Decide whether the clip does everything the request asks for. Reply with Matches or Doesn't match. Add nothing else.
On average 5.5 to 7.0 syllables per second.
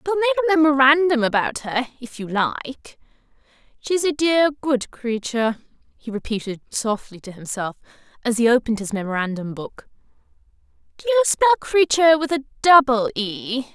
Matches